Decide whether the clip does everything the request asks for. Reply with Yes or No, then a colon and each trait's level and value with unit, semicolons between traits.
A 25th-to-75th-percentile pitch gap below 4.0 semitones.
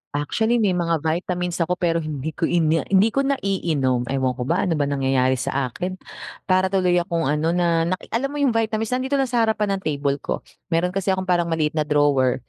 No: average, 4.8 semitones